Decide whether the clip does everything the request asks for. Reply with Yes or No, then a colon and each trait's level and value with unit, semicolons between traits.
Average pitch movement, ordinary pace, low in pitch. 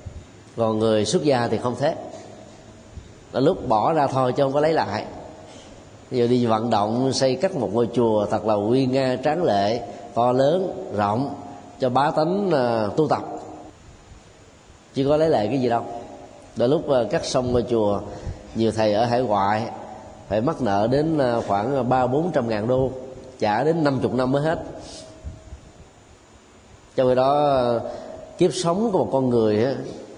Yes: average, 4.5 semitones; average, 180 wpm; low, 120 Hz